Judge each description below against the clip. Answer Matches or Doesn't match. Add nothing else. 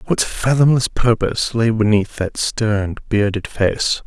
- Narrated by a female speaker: Doesn't match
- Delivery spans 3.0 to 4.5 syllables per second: Matches